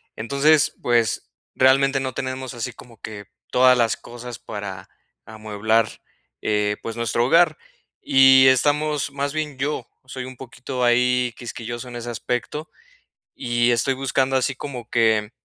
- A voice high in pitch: No, low, 125 Hz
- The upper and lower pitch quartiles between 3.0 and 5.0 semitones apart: No, narrow, 2.5 semitones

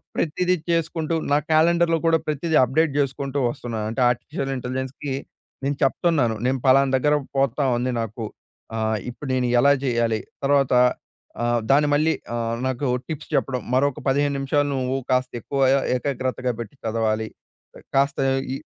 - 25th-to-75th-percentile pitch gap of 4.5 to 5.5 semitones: No, average, 2.9 semitones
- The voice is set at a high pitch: No, low, 135 Hz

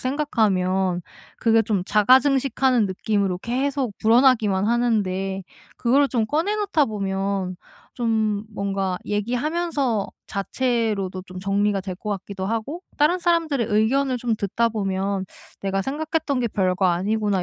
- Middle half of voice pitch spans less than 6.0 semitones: Yes, average, 5.1 semitones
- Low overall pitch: No, high, 220 Hz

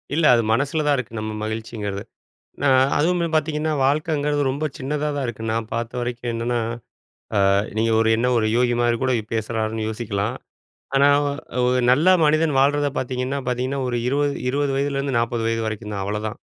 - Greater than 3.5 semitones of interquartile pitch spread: Yes, average, 4.0 semitones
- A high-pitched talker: No, low, 125 Hz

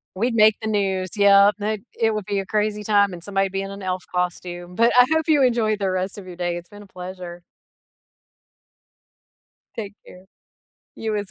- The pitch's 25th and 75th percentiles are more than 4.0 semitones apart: No, narrow, 2.5 semitones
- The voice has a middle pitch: No, high, 200 Hz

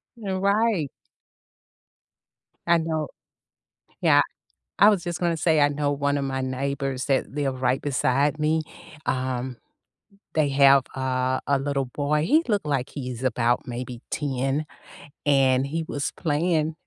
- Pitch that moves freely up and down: No, average, 3.2 semitones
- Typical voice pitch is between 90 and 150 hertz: Yes, medium, 140 Hz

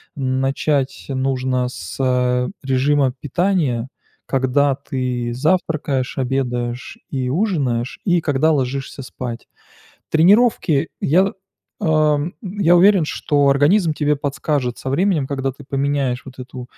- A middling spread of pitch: Yes, average, 3.3 semitones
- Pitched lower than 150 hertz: Yes, low, 135 Hz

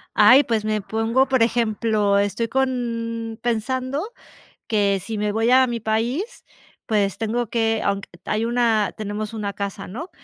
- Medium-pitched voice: No, high, 225 Hz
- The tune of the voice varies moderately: No, narrow, 2.3 semitones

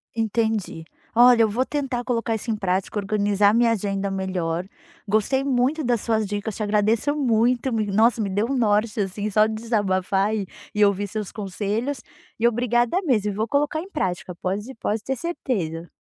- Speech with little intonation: No, average, 3.1 semitones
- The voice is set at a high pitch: Yes, high, 215 Hz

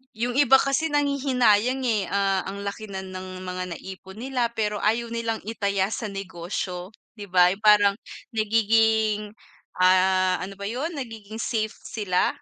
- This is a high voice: Yes, high, 210 Hz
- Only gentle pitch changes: No, average, 3.2 semitones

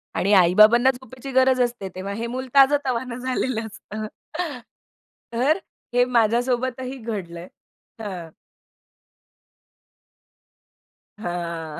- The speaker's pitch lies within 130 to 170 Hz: No, high, 235 Hz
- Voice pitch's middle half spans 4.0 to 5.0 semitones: Yes, average, 4.4 semitones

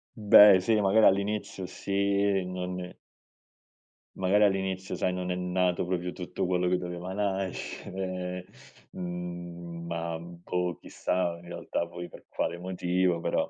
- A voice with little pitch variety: Yes, narrow, 1.5 semitones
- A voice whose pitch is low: Yes, very low, 90 Hz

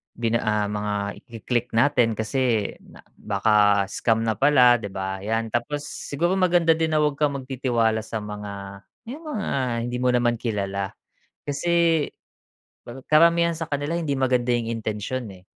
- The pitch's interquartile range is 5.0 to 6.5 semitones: Yes, average, 5.3 semitones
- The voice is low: Yes, low, 120 Hz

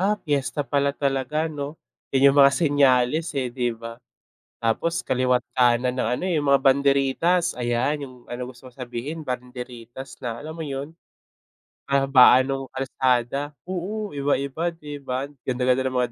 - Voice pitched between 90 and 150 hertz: Yes, low, 135 Hz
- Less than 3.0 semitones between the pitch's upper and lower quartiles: Yes, narrow, 2.6 semitones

